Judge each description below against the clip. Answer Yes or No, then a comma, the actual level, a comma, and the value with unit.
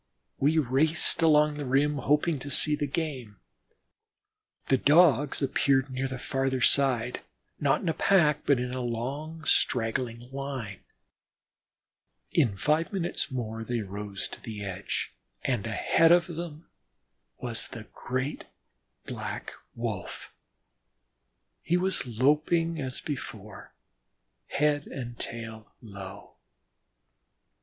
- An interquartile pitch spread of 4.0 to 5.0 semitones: Yes, average, 4.4 semitones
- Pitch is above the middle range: No, low, 135 Hz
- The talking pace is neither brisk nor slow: No, slow, 115 wpm